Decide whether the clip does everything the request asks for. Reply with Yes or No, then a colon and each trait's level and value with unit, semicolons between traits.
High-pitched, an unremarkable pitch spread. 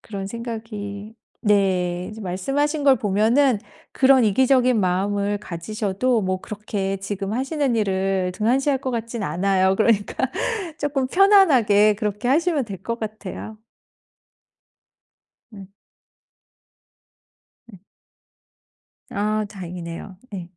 Yes: high, 210 Hz; average, 4.4 semitones